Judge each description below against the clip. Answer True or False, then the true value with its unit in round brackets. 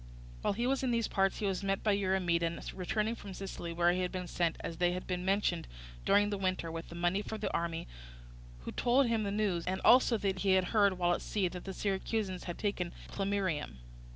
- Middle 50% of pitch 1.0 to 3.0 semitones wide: True (2.7 semitones)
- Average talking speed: False (220 wpm)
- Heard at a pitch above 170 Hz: True (190 Hz)